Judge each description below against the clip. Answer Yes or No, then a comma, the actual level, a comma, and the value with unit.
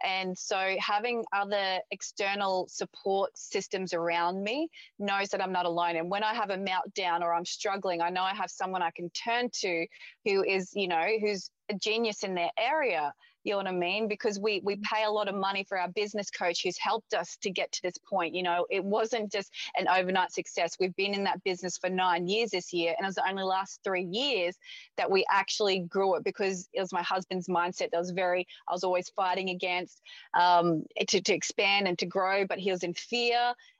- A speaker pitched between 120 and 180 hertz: No, high, 190 Hz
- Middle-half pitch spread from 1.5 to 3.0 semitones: Yes, narrow, 2.4 semitones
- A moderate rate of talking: No, fast, 220 wpm